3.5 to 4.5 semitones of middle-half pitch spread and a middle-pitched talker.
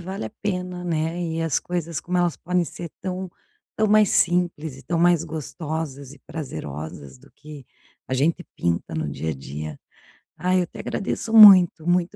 Yes: average, 4.1 semitones; medium, 170 Hz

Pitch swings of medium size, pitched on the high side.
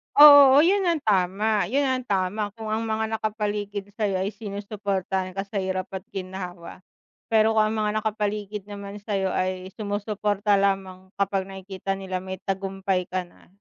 No: narrow, 2.2 semitones; high, 200 Hz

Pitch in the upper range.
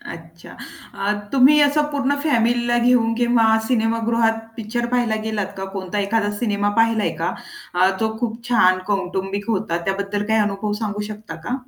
Yes: high, 220 Hz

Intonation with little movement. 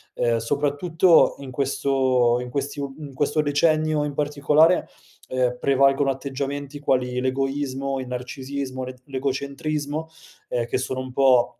Yes: narrow, 2.1 semitones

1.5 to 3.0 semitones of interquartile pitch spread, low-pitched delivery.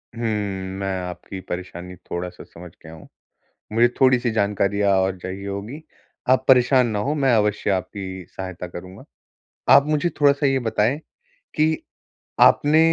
No: wide, 5.5 semitones; low, 100 Hz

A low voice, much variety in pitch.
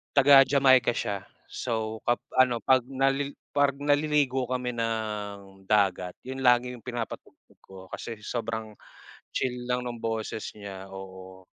No: low, 120 Hz; average, 4.1 semitones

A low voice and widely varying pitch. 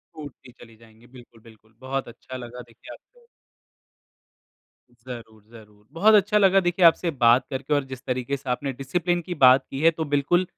Yes: low, 130 Hz; wide, 5.7 semitones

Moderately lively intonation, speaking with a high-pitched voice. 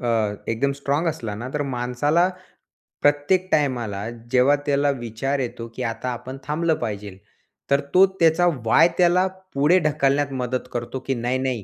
No: average, 3.8 semitones; low, 135 Hz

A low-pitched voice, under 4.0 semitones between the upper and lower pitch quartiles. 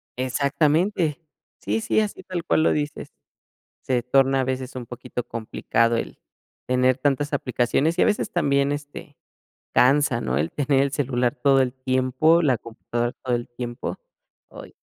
Yes: low, 130 Hz; average, 3.0 semitones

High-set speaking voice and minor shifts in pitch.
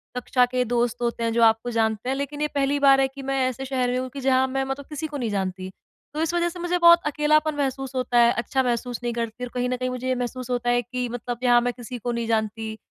Yes: very high, 250 Hz; narrow, 2.3 semitones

